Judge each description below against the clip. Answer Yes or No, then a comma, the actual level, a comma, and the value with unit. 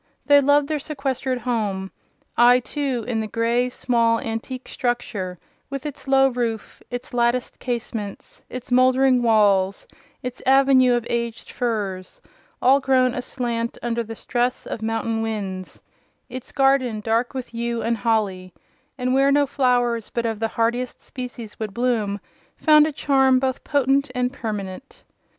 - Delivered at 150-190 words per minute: No, average, 140 wpm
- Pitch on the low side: No, high, 245 Hz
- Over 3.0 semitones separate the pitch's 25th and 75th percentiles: No, narrow, 2.6 semitones